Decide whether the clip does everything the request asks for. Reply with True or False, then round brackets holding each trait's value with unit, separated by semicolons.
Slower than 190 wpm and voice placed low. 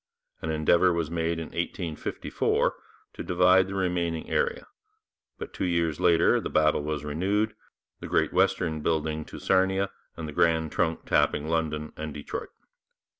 True (150 wpm; 80 Hz)